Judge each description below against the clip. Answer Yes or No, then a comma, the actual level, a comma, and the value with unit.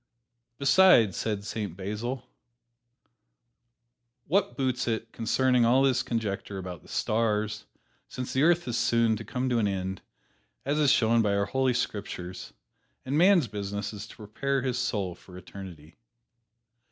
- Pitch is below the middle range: Yes, low, 115 Hz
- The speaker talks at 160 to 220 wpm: No, average, 145 wpm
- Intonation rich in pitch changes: No, average, 4.5 semitones